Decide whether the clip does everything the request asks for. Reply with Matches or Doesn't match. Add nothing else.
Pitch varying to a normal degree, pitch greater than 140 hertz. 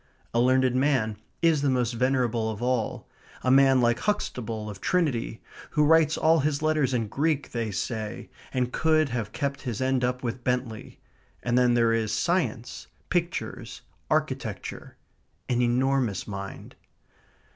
Doesn't match